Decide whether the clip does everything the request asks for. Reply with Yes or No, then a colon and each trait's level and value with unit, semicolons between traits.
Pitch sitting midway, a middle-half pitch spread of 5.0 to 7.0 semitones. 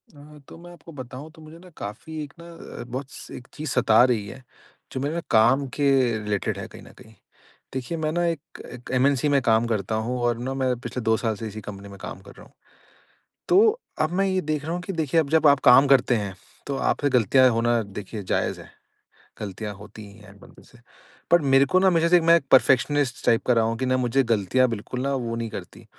No: low, 130 Hz; average, 5.3 semitones